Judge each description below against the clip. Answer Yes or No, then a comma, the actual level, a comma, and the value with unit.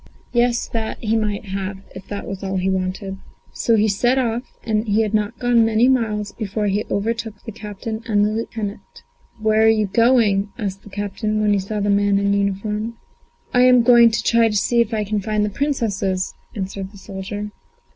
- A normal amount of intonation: No, narrow, 2.2 semitones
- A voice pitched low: No, high, 210 Hz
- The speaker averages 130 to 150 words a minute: No, average, 190 wpm